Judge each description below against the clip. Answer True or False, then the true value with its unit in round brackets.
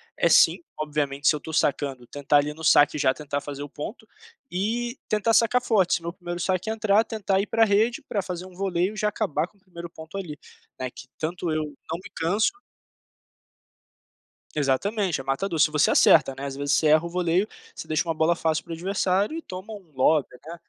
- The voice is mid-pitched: True (170 Hz)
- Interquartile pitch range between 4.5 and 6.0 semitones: True (4.8 semitones)